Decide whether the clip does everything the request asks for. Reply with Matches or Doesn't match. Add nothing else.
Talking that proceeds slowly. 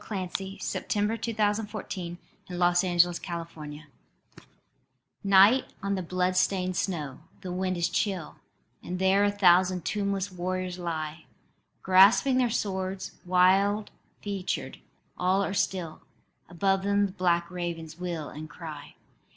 Matches